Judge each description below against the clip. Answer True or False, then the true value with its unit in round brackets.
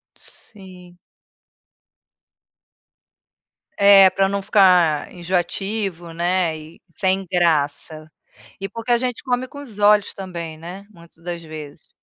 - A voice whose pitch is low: False (185 Hz)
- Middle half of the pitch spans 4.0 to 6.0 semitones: False (3.0 semitones)